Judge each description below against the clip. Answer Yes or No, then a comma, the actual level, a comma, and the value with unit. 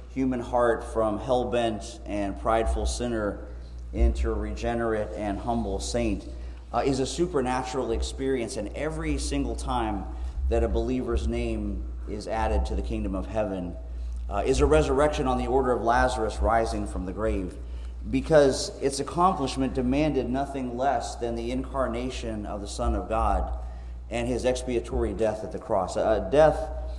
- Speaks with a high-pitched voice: No, low, 115 Hz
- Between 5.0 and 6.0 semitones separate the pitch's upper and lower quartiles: Yes, average, 5.3 semitones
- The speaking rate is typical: Yes, average, 155 wpm